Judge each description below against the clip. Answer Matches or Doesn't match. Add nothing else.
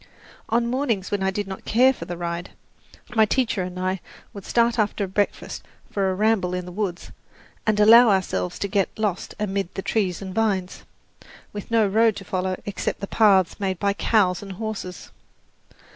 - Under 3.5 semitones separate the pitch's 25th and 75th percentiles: Matches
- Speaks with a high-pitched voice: Matches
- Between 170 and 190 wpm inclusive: Matches